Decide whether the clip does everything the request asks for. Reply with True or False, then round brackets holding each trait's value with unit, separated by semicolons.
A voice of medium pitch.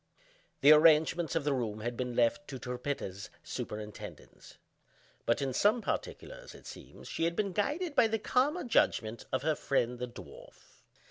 True (145 Hz)